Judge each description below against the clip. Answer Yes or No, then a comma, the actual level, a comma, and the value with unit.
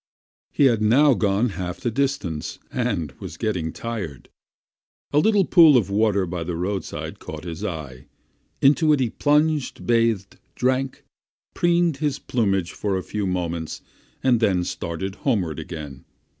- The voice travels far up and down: Yes, wide, 7.1 semitones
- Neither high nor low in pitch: No, low, 105 Hz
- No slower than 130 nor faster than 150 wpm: Yes, average, 145 wpm